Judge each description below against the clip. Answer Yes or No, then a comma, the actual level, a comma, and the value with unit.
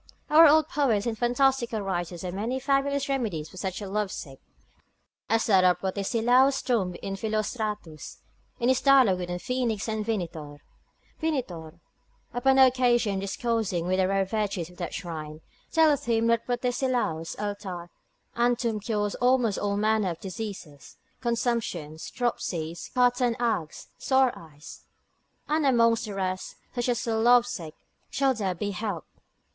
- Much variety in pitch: No, average, 4.9 semitones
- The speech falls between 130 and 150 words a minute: Yes, average, 145 wpm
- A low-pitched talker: No, high, 220 Hz